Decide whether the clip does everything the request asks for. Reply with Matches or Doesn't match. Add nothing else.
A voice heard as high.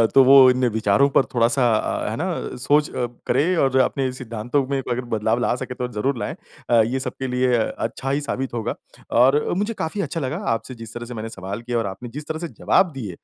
Doesn't match